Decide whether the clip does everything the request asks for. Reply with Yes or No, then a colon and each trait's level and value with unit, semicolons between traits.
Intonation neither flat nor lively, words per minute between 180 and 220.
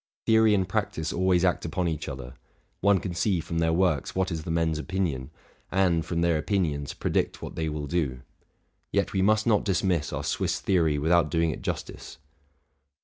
Yes: average, 3.2 semitones; average, 185 wpm